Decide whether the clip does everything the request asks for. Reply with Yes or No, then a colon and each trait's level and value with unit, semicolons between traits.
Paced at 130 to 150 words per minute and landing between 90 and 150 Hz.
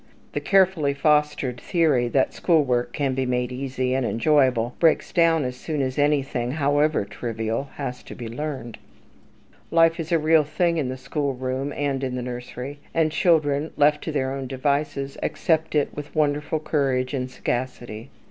No: average, 170 wpm; medium, 140 Hz